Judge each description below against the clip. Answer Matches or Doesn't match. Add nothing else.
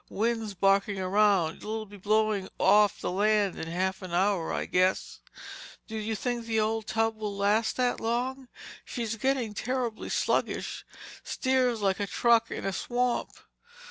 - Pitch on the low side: Doesn't match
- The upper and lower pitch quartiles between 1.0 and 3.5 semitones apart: Matches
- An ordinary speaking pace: Matches